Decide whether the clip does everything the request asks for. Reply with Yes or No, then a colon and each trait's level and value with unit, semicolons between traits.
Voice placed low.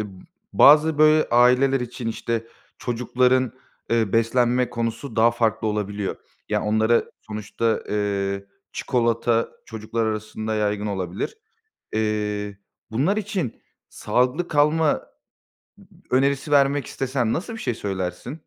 Yes: low, 115 Hz